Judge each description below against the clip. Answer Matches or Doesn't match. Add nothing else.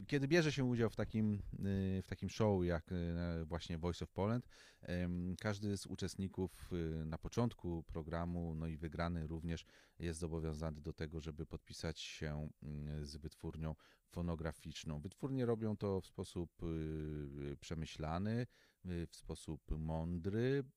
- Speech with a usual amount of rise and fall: Matches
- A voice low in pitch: Matches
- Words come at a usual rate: Matches